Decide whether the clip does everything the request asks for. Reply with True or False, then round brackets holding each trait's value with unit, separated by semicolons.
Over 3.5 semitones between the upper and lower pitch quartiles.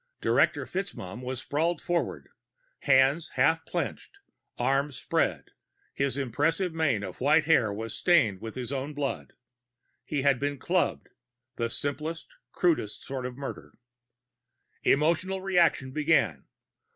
True (4.2 semitones)